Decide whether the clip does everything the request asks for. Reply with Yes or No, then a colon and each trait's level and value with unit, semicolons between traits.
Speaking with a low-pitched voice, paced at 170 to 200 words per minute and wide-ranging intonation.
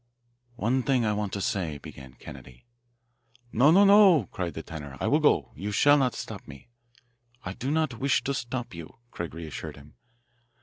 Yes: low, 105 Hz; average, 175 wpm; wide, 8.9 semitones